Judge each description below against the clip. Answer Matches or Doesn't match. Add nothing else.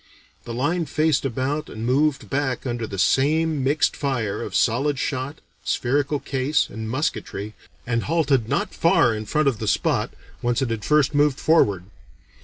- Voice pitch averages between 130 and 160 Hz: Matches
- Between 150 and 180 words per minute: Matches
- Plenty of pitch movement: Doesn't match